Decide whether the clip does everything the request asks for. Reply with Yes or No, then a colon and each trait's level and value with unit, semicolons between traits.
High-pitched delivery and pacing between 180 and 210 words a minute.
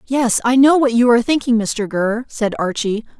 Yes: high, 235 Hz; fast, 205 wpm